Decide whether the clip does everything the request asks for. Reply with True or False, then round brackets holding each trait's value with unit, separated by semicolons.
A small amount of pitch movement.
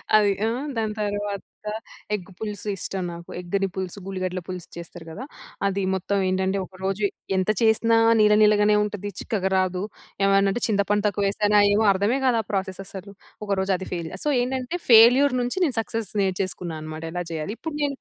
True (2.3 semitones)